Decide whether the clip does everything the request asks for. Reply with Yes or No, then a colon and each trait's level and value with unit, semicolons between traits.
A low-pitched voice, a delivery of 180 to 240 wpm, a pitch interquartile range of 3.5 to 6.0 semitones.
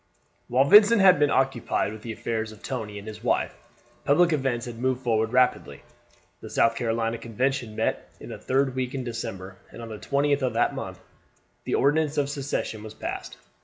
Yes: low, 125 Hz; average, 190 wpm; average, 3.9 semitones